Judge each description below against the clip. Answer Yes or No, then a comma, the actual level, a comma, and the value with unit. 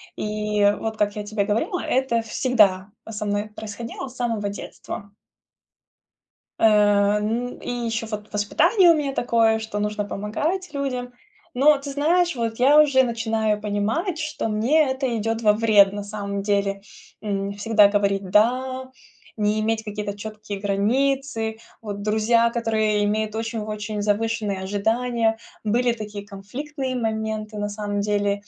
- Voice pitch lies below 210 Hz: No, high, 220 Hz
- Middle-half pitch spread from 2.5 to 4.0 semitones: Yes, average, 2.8 semitones